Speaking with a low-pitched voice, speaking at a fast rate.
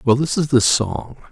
Yes: low, 130 Hz; fast, 230 wpm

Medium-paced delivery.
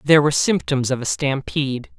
Yes: average, 180 wpm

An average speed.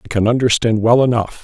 No: fast, 210 wpm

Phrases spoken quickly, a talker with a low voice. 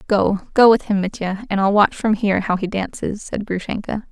No: fast, 220 wpm; high, 205 Hz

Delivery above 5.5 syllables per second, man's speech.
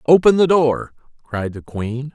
No: 4.1 syllables/s; male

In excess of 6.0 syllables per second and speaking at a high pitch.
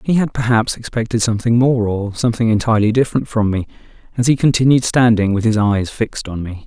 No: 6.3 syllables/s; low, 115 Hz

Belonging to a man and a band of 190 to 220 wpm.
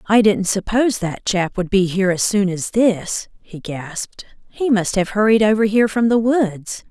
No: female; average, 200 wpm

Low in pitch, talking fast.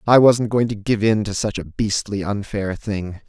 Yes: low, 105 Hz; fast, 220 wpm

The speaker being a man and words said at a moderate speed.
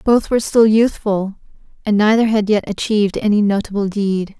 No: female; average, 165 wpm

